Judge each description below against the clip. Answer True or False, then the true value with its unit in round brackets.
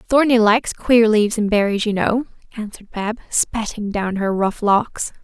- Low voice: False (215 Hz)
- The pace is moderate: True (170 wpm)